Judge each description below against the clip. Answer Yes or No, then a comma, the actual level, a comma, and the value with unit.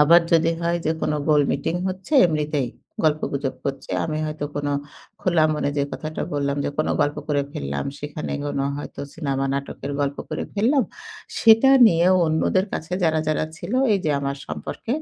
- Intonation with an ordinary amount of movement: Yes, average, 3.0 semitones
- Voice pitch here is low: No, medium, 155 Hz